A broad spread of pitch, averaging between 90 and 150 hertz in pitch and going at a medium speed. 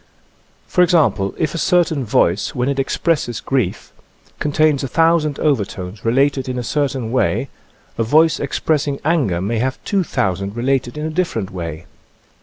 Yes: wide, 5.8 semitones; low, 135 Hz; average, 150 wpm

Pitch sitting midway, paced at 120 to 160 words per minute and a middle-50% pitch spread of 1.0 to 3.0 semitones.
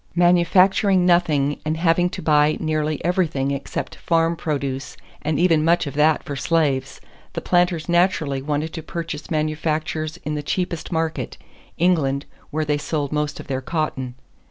Yes: medium, 155 Hz; average, 155 wpm; narrow, 2.5 semitones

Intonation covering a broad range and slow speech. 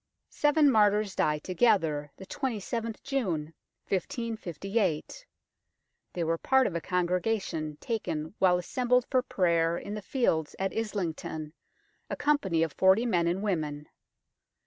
Yes: wide, 5.8 semitones; slow, 125 wpm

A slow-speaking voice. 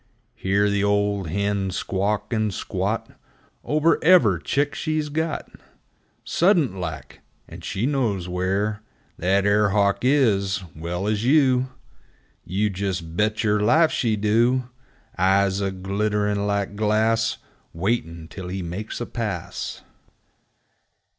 Yes: slow, 120 wpm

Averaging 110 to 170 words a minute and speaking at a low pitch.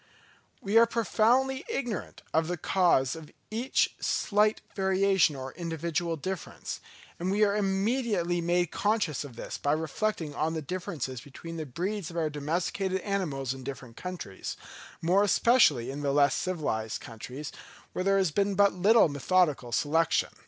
No: average, 150 wpm; medium, 175 Hz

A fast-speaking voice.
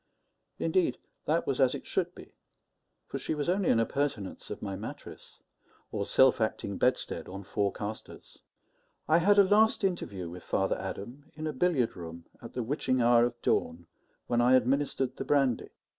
No: average, 175 wpm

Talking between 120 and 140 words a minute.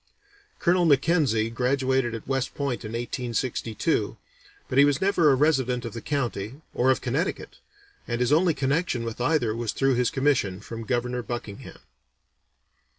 No: average, 155 wpm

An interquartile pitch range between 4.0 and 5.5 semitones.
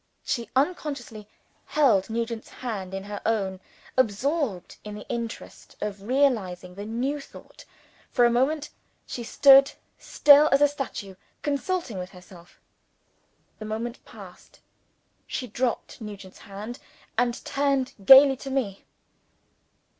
Yes: average, 5.2 semitones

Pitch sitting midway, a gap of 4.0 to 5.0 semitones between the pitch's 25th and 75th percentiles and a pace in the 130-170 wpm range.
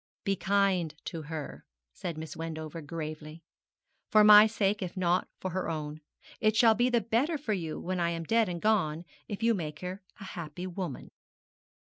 No: medium, 180 Hz; average, 4.7 semitones; average, 185 wpm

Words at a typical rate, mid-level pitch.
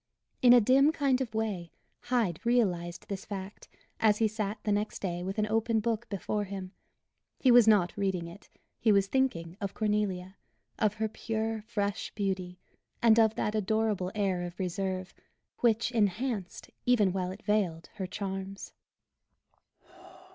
No: average, 155 wpm; high, 205 Hz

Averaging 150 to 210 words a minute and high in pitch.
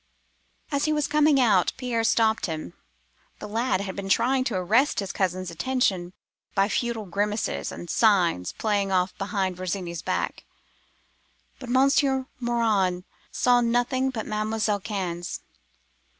No: slow, 135 wpm; high, 215 Hz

